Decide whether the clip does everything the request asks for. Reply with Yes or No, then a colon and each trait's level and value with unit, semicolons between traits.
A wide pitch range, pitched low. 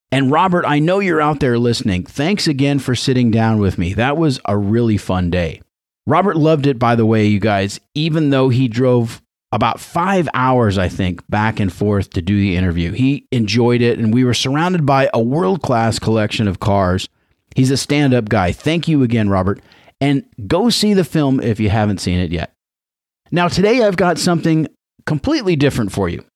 Yes: wide, 6.4 semitones; low, 120 Hz